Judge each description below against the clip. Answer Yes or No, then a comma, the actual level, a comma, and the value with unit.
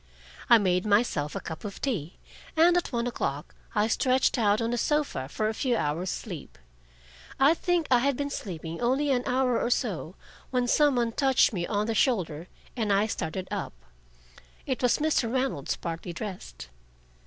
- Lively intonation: Yes, wide, 6.2 semitones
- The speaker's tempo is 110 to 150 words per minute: No, average, 175 wpm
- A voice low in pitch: No, high, 230 Hz